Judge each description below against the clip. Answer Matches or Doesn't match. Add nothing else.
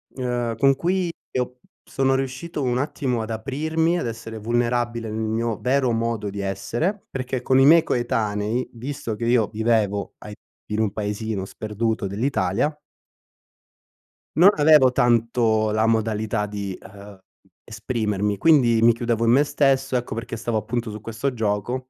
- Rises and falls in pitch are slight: Doesn't match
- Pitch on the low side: Matches